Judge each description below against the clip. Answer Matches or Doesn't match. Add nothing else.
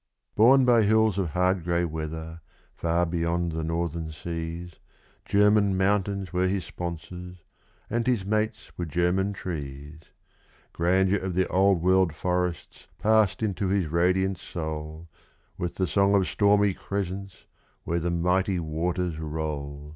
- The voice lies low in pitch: Matches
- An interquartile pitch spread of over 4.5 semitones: Doesn't match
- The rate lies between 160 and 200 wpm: Doesn't match